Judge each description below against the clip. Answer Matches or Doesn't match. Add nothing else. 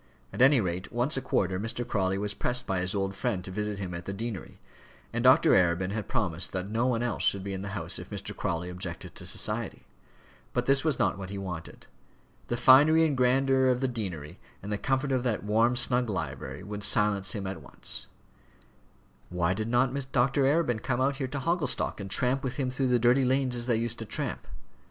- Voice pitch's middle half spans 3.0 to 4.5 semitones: Doesn't match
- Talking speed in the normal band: Doesn't match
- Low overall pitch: Matches